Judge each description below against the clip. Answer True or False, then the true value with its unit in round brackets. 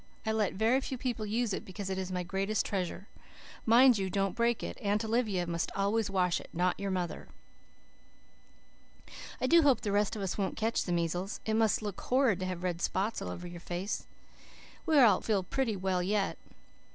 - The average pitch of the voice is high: True (200 Hz)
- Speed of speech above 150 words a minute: True (200 wpm)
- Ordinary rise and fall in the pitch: True (3.4 semitones)